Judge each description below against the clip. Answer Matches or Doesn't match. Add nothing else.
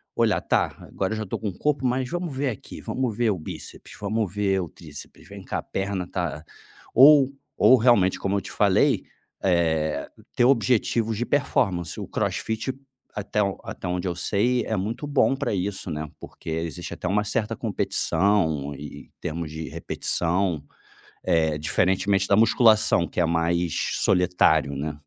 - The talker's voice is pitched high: Doesn't match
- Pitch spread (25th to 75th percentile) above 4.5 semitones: Matches